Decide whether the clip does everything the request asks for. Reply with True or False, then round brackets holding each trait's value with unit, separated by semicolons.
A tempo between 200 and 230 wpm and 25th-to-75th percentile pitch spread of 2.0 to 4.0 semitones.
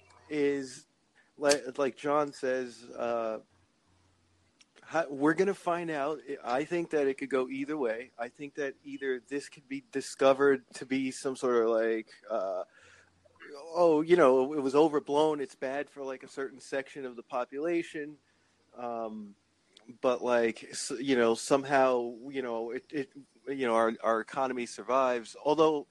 False (155 wpm; 3.3 semitones)